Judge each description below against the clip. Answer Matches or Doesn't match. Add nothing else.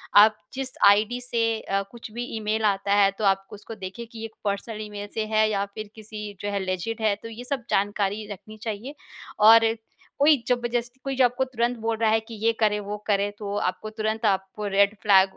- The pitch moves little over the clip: Matches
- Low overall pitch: Doesn't match